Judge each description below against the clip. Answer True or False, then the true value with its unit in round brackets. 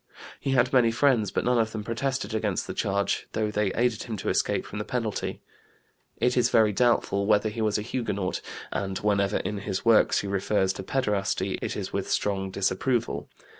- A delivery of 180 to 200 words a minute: True (195 wpm)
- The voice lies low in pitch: True (105 Hz)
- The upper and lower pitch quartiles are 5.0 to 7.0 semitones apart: False (3.0 semitones)